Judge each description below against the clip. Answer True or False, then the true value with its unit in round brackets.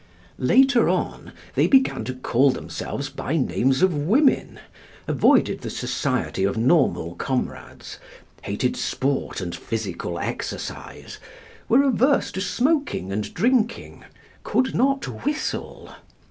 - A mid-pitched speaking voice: True (165 Hz)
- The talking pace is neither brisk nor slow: False (115 wpm)